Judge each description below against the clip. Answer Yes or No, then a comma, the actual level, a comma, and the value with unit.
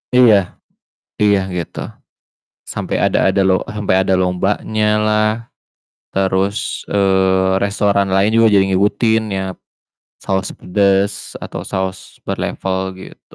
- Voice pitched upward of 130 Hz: No, very low, 95 Hz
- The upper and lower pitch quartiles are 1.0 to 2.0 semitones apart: Yes, narrow, 1.5 semitones